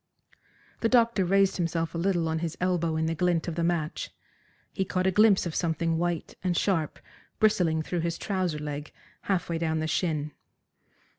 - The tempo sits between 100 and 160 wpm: No, average, 180 wpm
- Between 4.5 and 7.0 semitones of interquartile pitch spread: No, narrow, 2.5 semitones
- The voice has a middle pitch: Yes, medium, 170 Hz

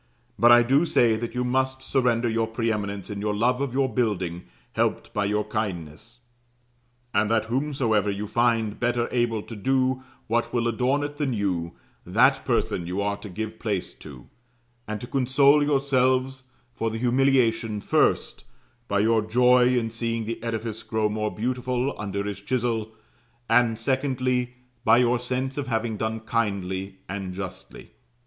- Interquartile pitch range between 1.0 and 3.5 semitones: Yes, average, 3.1 semitones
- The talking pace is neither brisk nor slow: Yes, average, 160 wpm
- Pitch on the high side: No, low, 115 Hz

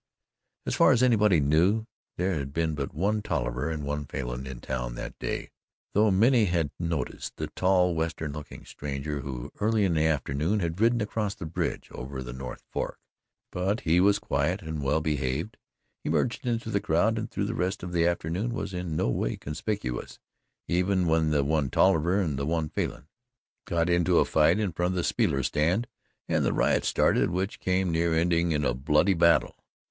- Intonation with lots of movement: No, average, 4.7 semitones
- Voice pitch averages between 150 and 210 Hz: No, very low, 85 Hz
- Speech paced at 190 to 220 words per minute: Yes, average, 195 wpm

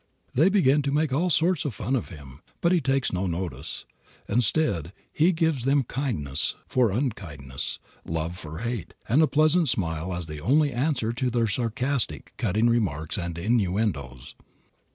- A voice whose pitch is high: No, low, 115 Hz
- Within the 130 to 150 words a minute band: No, average, 160 wpm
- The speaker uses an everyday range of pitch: No, wide, 8.7 semitones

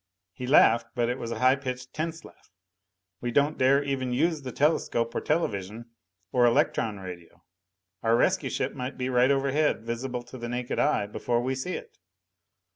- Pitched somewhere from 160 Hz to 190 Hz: No, low, 125 Hz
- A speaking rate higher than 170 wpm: Yes, average, 180 wpm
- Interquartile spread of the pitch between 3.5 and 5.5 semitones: No, average, 2.8 semitones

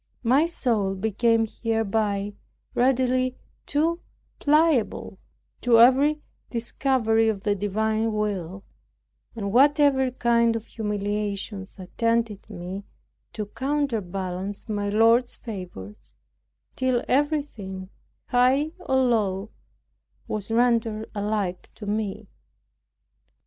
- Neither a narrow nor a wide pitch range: Yes, average, 3.8 semitones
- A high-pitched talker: Yes, high, 225 Hz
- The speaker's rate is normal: No, slow, 90 wpm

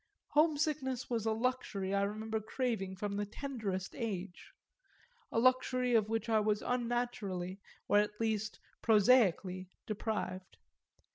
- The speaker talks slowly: Yes, slow, 125 wpm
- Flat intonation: No, average, 3.7 semitones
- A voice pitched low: No, high, 220 Hz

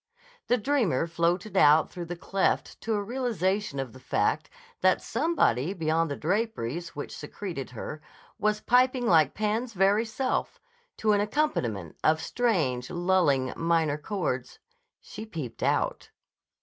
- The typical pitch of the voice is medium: Yes, medium, 175 Hz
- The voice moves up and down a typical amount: No, wide, 6.4 semitones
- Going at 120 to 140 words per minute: Yes, slow, 135 wpm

